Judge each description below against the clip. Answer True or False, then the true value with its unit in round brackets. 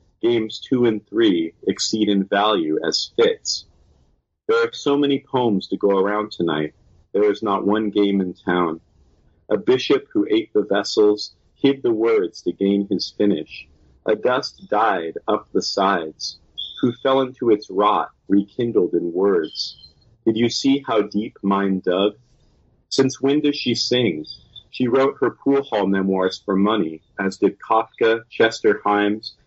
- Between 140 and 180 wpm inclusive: True (155 wpm)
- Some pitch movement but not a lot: False (6.1 semitones)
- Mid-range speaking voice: False (110 Hz)